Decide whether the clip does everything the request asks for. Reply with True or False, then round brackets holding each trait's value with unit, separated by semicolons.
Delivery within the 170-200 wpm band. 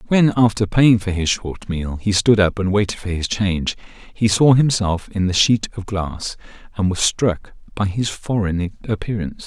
True (190 wpm)